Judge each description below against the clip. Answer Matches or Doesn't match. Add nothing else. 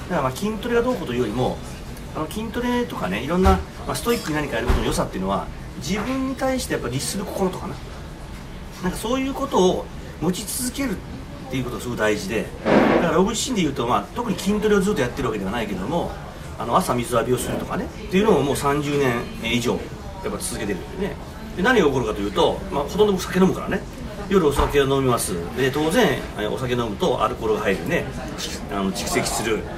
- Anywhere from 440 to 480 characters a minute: Matches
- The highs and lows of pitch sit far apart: Matches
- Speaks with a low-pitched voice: Doesn't match